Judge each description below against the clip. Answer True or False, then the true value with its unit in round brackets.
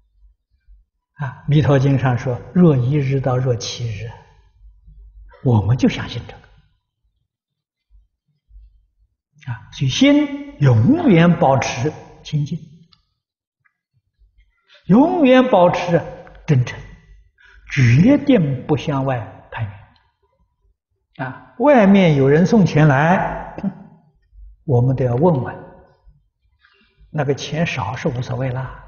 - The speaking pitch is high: False (135 Hz)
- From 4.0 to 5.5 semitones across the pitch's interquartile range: False (6.3 semitones)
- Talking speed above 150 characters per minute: False (135 characters per minute)